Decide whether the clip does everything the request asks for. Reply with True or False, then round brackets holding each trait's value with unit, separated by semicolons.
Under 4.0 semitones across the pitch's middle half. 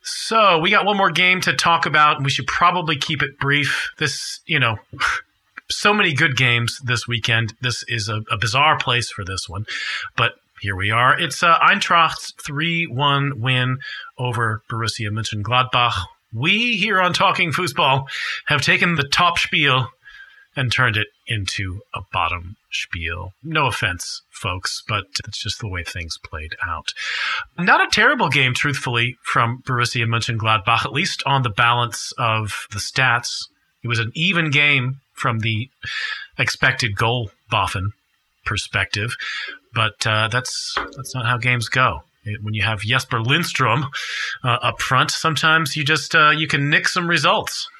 False (5.2 semitones)